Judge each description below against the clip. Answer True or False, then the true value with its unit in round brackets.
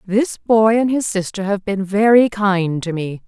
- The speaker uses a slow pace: False (200 wpm)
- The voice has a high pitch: True (200 Hz)